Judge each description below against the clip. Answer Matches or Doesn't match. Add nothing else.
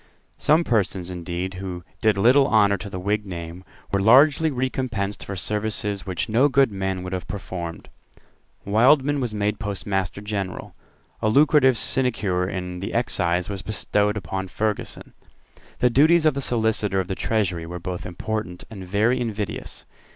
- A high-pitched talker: Doesn't match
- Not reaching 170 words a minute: Matches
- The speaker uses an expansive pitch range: Doesn't match